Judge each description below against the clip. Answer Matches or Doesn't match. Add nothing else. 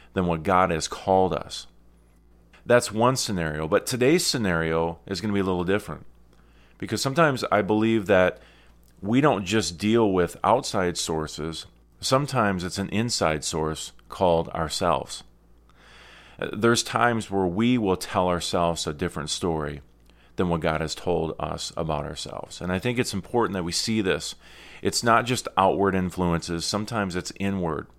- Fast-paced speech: Doesn't match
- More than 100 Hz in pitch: Doesn't match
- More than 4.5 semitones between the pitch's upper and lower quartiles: Matches